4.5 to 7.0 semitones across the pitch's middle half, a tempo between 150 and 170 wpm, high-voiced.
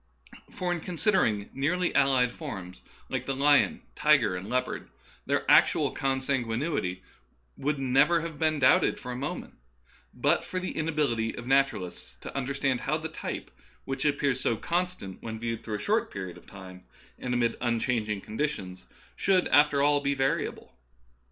No: average, 4.9 semitones; average, 160 wpm; low, 135 Hz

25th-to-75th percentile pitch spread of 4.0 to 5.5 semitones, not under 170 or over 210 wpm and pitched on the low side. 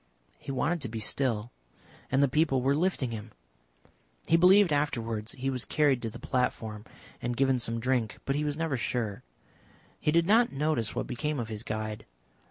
Yes: average, 4.7 semitones; average, 180 wpm; low, 130 Hz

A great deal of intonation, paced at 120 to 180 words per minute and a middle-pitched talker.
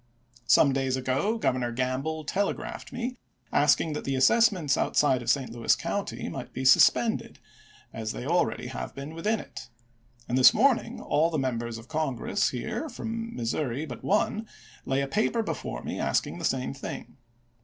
Yes: wide, 8.5 semitones; average, 170 wpm; medium, 145 Hz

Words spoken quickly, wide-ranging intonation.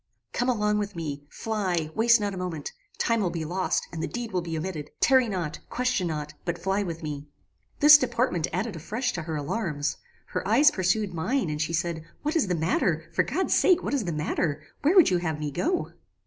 Yes: fast, 215 wpm; wide, 6.2 semitones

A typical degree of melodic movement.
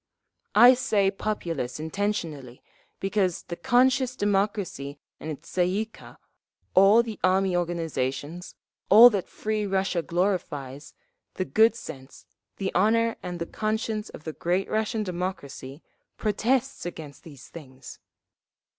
Yes: average, 4.8 semitones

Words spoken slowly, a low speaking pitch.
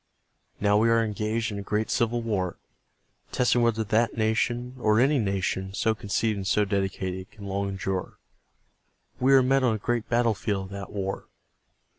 No: average, 170 wpm; low, 105 Hz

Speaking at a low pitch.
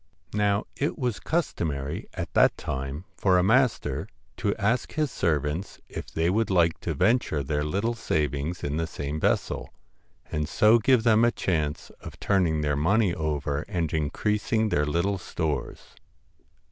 Yes: very low, 85 Hz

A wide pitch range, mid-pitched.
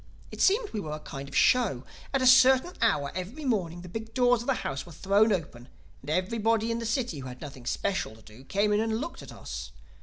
No: wide, 8.0 semitones; high, 210 Hz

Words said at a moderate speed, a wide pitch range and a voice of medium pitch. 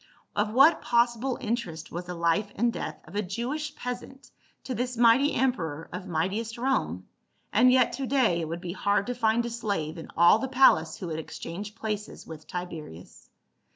No: average, 190 wpm; wide, 6.3 semitones; high, 215 Hz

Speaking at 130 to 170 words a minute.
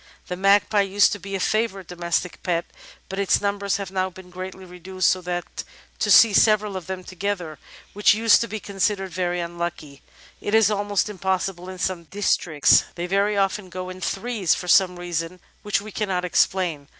No: average, 185 wpm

